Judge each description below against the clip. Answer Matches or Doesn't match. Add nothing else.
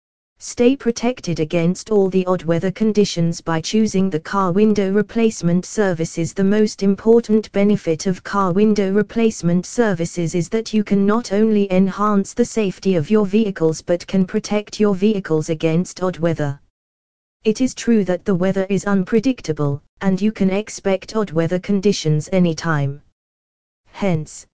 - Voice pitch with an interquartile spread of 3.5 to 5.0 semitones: Matches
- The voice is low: Doesn't match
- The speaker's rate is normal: Matches